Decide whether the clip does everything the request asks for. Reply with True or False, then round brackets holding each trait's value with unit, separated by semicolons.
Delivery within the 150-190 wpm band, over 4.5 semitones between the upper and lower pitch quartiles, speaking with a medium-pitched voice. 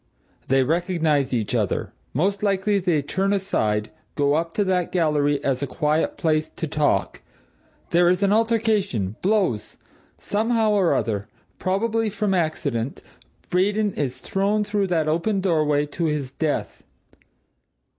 False (135 wpm; 5.5 semitones; 170 Hz)